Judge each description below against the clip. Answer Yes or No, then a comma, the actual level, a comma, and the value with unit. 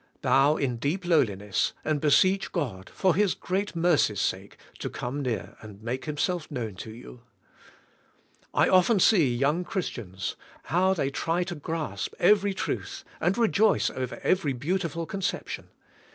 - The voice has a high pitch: No, medium, 150 Hz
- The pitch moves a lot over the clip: Yes, wide, 7.1 semitones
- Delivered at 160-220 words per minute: No, average, 145 wpm